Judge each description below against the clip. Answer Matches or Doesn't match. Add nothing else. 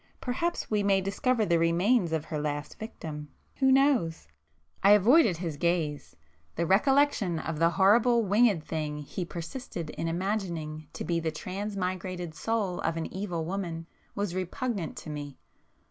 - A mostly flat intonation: Doesn't match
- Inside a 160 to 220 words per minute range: Doesn't match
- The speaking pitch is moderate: Matches